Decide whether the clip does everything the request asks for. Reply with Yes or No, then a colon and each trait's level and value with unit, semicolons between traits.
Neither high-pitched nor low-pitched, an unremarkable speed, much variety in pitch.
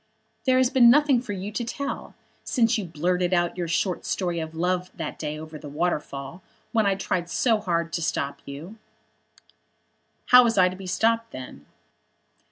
Yes: medium, 180 Hz; average, 175 wpm; wide, 5.7 semitones